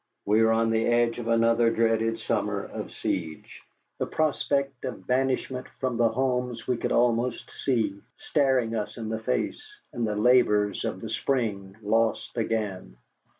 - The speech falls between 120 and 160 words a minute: Yes, average, 155 wpm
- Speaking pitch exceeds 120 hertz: No, low, 115 Hz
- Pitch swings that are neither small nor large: No, narrow, 2.3 semitones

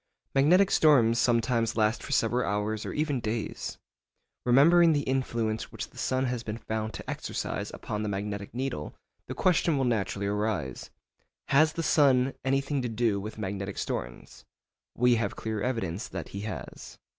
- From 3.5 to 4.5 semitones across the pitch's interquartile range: Yes, average, 4.1 semitones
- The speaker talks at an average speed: Yes, average, 160 wpm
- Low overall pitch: Yes, low, 115 Hz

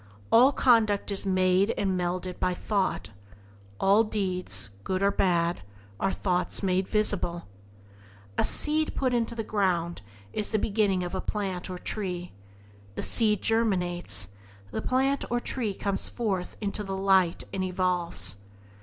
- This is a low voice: No, high, 195 Hz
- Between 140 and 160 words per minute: Yes, average, 145 wpm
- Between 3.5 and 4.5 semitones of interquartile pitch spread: No, average, 3.0 semitones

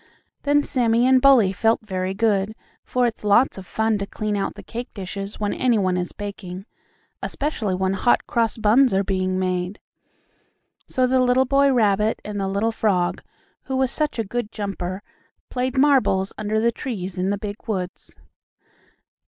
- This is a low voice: No, high, 210 Hz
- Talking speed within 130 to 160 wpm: No, average, 170 wpm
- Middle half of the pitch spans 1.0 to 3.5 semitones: No, average, 4.2 semitones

